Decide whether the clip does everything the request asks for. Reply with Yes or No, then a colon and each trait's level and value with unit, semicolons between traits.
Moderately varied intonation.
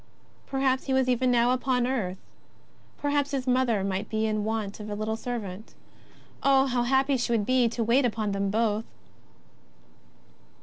Yes: average, 3.4 semitones